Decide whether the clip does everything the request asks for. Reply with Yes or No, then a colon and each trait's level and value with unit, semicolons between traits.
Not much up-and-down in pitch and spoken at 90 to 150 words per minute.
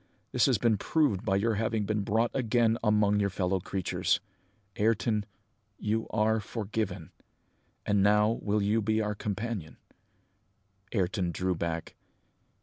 Yes: narrow, 2.3 semitones; slow, 135 wpm